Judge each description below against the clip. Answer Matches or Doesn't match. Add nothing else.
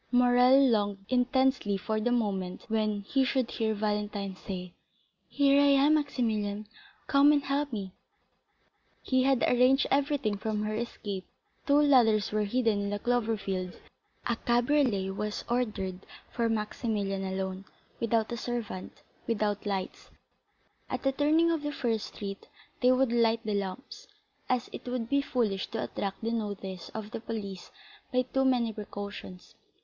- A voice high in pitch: Matches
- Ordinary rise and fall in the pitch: Matches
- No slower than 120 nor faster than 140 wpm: Doesn't match